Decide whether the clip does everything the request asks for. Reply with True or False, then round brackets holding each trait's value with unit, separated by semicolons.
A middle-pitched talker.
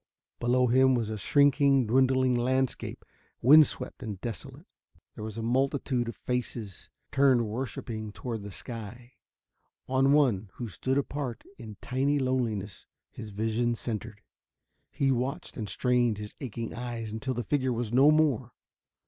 False (120 Hz)